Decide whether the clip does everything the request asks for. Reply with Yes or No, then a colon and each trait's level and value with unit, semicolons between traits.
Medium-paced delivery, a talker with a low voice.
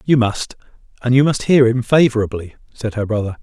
Yes: average, 190 wpm; low, 120 Hz